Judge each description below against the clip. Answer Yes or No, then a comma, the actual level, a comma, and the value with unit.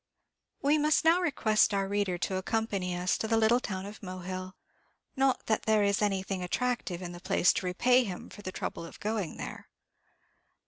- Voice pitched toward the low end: No, high, 200 Hz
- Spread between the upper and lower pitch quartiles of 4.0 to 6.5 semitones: No, average, 3.4 semitones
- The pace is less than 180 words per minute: No, average, 185 wpm